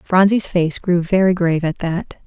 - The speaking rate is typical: Yes, average, 185 wpm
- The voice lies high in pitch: No, medium, 175 Hz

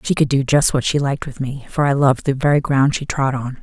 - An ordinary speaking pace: No, fast, 300 wpm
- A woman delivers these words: Yes, female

